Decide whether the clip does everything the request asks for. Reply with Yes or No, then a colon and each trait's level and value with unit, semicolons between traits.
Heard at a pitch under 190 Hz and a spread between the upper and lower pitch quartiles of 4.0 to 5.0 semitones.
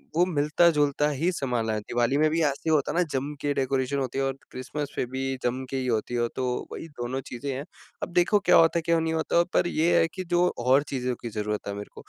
Yes: medium, 140 Hz; average, 4.3 semitones